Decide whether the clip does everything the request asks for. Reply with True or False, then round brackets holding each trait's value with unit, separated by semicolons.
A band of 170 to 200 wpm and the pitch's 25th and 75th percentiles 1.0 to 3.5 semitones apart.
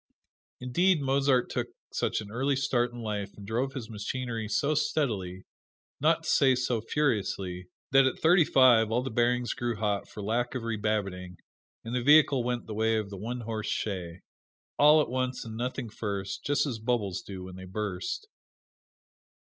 False (175 wpm; 4.1 semitones)